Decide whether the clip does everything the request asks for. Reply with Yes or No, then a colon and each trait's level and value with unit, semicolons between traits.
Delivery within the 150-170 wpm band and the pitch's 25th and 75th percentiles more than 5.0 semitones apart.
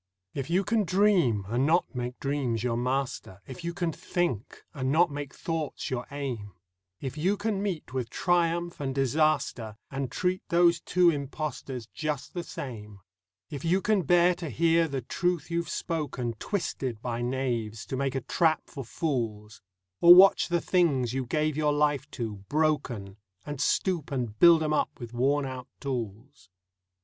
Yes: average, 165 wpm; wide, 5.4 semitones